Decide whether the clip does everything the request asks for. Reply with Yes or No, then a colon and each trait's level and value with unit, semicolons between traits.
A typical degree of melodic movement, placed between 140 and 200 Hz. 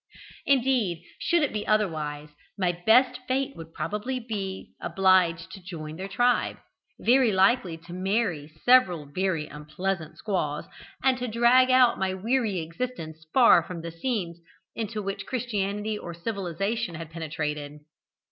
No: wide, 6.1 semitones; high, 190 Hz